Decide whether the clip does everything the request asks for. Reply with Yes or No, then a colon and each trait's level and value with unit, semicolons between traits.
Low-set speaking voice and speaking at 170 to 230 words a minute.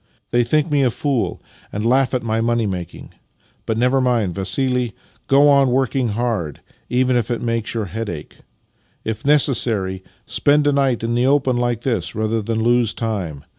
Yes: low, 120 Hz; average, 180 wpm